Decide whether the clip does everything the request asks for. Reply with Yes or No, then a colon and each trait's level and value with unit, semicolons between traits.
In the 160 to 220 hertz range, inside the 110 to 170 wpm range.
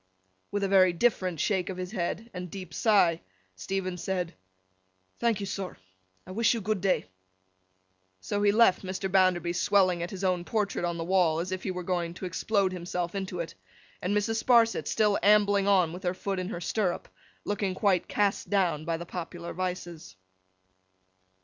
No: medium, 185 Hz; average, 180 wpm